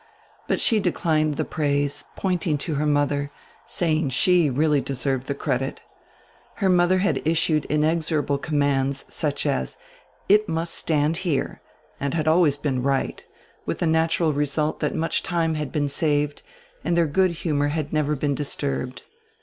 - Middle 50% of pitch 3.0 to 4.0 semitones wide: No, narrow, 2.5 semitones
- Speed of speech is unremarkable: Yes, average, 155 wpm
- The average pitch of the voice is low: No, medium, 150 Hz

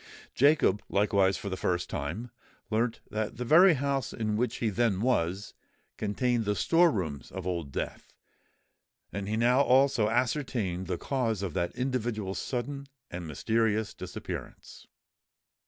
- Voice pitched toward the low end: Yes, low, 110 Hz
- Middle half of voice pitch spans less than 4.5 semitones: No, average, 4.8 semitones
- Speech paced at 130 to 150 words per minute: Yes, average, 140 wpm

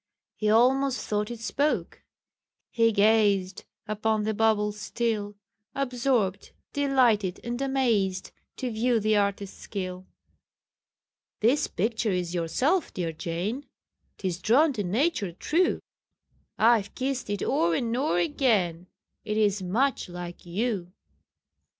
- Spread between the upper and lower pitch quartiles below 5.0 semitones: Yes, average, 4.5 semitones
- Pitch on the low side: No, high, 215 Hz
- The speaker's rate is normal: No, slow, 120 wpm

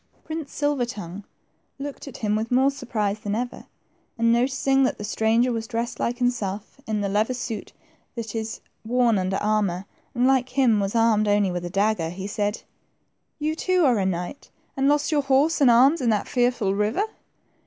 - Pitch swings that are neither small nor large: Yes, average, 4.1 semitones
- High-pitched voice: Yes, high, 230 Hz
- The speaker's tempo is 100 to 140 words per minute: No, average, 185 wpm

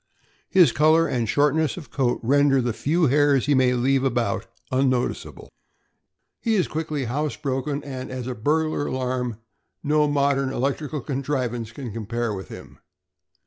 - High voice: No, low, 135 Hz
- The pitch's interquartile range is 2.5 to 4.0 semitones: Yes, average, 3.0 semitones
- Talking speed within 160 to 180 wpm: No, average, 145 wpm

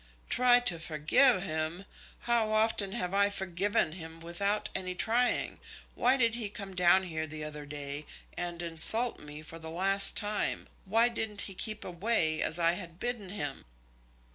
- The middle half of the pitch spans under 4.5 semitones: No, average, 4.9 semitones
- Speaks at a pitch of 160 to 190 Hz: Yes, medium, 185 Hz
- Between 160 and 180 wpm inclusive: Yes, average, 165 wpm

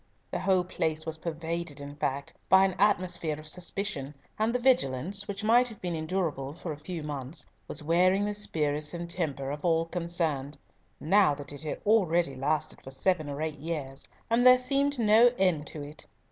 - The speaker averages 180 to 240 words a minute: Yes, average, 190 wpm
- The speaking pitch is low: No, medium, 165 Hz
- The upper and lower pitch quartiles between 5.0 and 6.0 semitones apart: No, average, 4.6 semitones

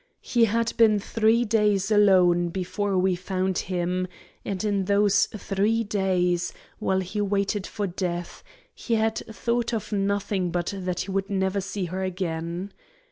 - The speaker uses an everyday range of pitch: No, narrow, 2.3 semitones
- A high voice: Yes, high, 195 Hz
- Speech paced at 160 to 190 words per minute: No, average, 150 wpm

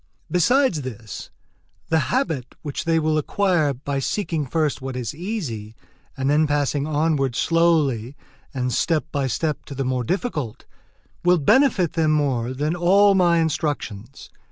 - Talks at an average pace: Yes, average, 145 wpm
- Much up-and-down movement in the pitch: No, average, 4.3 semitones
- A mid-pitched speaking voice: Yes, medium, 150 Hz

